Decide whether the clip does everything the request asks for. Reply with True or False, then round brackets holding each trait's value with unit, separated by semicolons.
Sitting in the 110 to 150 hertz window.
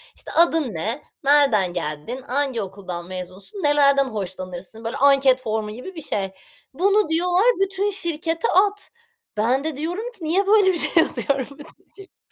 False (280 Hz)